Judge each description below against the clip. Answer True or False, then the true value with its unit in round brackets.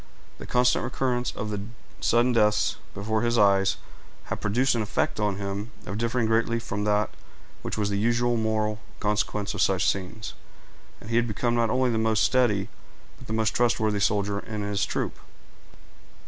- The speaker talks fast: False (165 wpm)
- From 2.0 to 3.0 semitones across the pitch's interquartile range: True (2.4 semitones)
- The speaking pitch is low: True (110 Hz)